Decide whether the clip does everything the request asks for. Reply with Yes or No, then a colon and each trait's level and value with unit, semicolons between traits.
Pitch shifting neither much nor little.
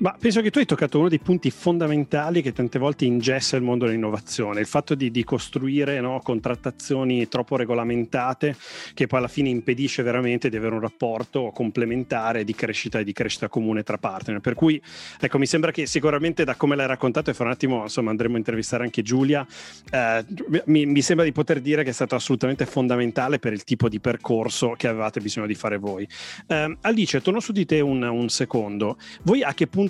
Yes: average, 4.1 semitones